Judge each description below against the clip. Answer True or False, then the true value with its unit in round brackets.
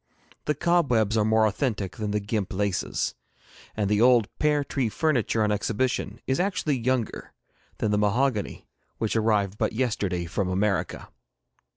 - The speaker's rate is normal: True (150 wpm)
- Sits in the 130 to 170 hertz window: False (110 Hz)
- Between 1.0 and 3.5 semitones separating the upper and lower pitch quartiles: False (3.9 semitones)